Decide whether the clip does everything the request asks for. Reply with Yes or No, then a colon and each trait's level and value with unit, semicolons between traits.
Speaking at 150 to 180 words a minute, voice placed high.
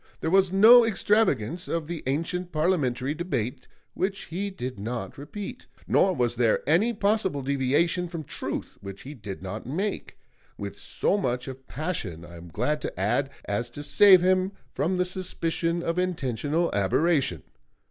No: average, 160 wpm; medium, 155 Hz